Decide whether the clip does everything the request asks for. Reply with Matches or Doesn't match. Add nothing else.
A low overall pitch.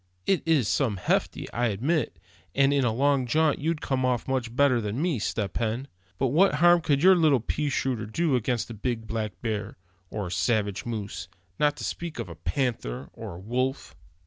Matches